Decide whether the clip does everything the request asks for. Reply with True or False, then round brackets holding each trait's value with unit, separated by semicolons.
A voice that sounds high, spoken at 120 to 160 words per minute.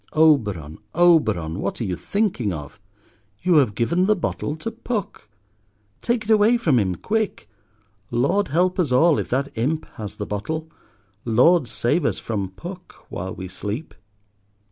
False (140 Hz; 155 wpm)